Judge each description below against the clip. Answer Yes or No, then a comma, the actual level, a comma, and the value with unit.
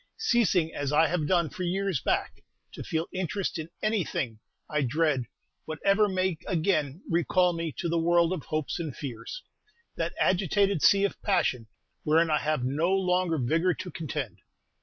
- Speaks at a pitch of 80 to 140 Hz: No, medium, 170 Hz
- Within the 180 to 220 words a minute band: No, average, 160 wpm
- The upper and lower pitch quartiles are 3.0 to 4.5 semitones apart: Yes, average, 3.6 semitones